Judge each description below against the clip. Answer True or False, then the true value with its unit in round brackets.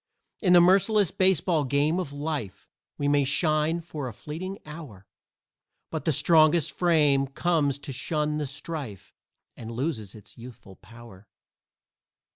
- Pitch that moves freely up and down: False (4.5 semitones)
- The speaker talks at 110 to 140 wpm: True (135 wpm)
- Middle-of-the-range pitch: True (150 Hz)